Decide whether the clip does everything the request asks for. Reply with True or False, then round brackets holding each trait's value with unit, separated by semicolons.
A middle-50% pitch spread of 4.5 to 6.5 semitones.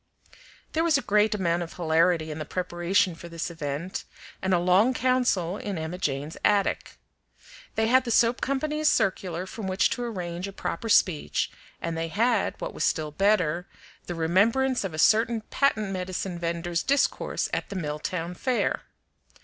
True (4.8 semitones)